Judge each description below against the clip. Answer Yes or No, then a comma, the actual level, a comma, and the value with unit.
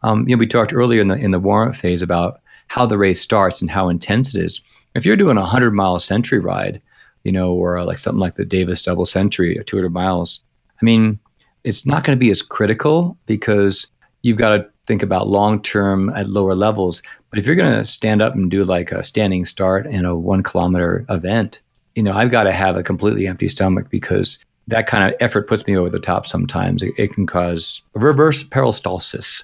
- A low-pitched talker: Yes, low, 100 Hz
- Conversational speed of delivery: No, fast, 215 wpm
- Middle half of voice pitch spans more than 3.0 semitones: Yes, average, 3.6 semitones